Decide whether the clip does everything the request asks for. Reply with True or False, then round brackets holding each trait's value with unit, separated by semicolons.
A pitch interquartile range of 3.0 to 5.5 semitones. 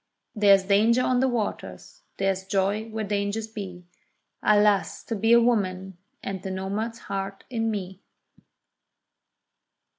False (2.6 semitones)